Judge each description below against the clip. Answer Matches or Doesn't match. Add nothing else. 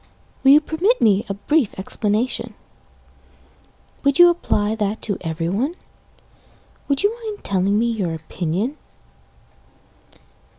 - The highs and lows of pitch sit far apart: Matches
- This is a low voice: Doesn't match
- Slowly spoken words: Matches